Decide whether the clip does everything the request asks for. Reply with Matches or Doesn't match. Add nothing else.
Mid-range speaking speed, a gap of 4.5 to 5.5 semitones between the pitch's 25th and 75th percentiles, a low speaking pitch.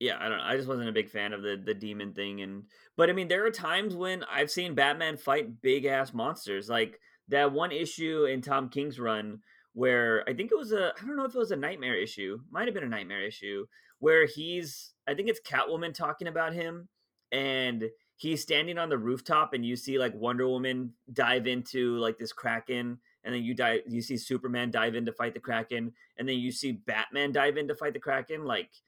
Doesn't match